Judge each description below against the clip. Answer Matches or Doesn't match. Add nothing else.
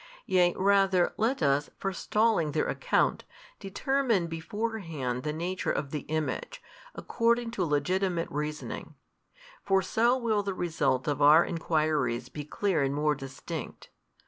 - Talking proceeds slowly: Matches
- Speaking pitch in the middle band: Matches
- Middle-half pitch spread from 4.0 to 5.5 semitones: Matches